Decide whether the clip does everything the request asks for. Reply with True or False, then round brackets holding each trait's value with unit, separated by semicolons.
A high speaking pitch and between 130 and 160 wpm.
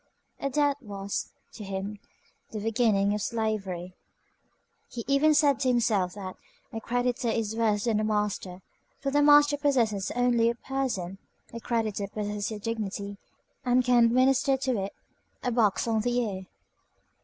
True (225 Hz; 155 wpm)